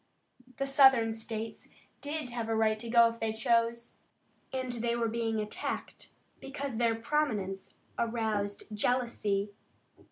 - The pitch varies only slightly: Yes, narrow, 1.8 semitones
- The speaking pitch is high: Yes, high, 230 Hz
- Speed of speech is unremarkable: No, slow, 130 wpm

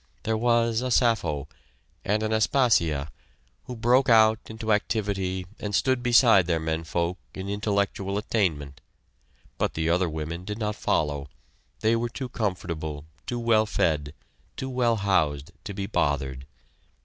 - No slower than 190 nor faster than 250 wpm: No, average, 145 wpm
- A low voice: Yes, low, 100 Hz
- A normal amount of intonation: No, wide, 5.9 semitones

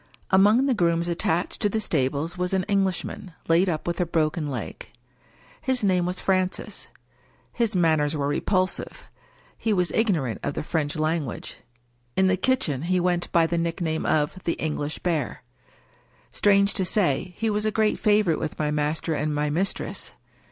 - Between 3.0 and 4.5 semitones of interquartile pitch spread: Yes, average, 3.8 semitones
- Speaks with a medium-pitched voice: Yes, medium, 175 Hz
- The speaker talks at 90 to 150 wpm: No, average, 175 wpm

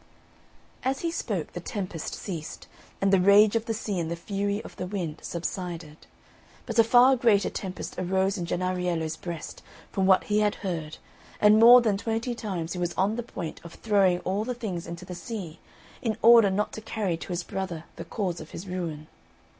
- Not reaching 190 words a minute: No, average, 195 wpm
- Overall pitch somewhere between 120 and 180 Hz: No, high, 190 Hz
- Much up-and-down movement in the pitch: No, average, 3.9 semitones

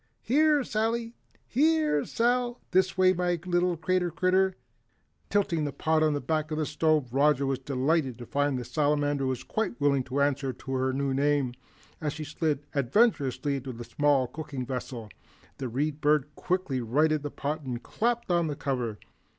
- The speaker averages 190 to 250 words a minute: No, average, 170 wpm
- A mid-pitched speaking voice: Yes, medium, 150 Hz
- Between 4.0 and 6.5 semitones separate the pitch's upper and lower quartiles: Yes, average, 4.8 semitones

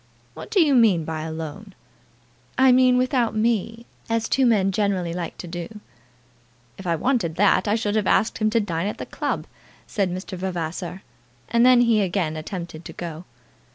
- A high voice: Yes, high, 200 Hz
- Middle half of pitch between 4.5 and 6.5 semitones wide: Yes, average, 4.9 semitones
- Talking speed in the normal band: Yes, average, 180 wpm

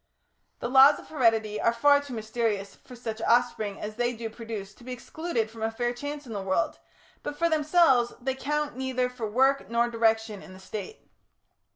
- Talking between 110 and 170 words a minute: No, average, 195 wpm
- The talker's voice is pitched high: Yes, high, 235 Hz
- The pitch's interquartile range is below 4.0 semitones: Yes, average, 3.3 semitones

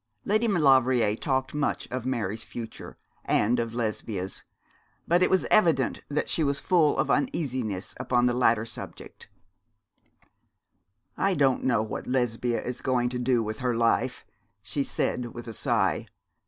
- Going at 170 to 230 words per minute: No, average, 150 wpm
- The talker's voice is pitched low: Yes, low, 125 Hz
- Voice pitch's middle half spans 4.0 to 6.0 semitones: No, average, 3.2 semitones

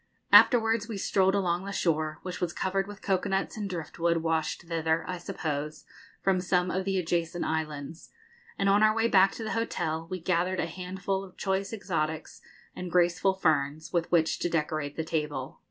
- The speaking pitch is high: No, medium, 180 Hz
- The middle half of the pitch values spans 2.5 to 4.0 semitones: Yes, average, 3.2 semitones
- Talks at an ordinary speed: Yes, average, 185 wpm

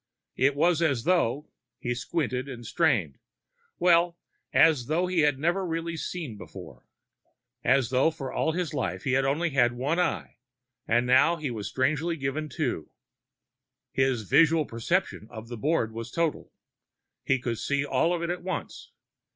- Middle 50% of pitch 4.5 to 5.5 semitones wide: Yes, average, 5.1 semitones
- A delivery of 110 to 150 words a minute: No, average, 165 wpm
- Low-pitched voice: No, medium, 145 Hz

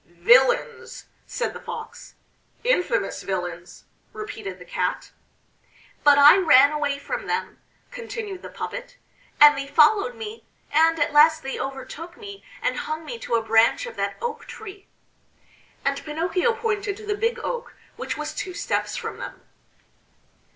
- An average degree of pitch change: No, wide, 7.9 semitones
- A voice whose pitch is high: Yes, very high, 335 Hz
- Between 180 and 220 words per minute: No, average, 150 wpm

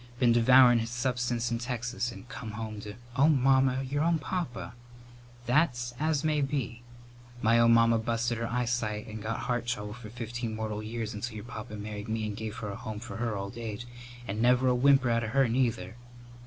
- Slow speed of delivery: No, fast, 205 wpm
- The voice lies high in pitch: No, low, 120 Hz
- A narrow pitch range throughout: Yes, narrow, 2.2 semitones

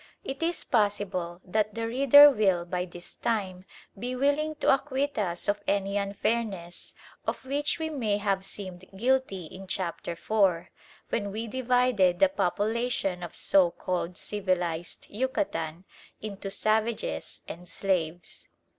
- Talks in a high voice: Yes, high, 205 Hz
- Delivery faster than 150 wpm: No, slow, 135 wpm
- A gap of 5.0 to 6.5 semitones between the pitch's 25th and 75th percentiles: Yes, wide, 5.5 semitones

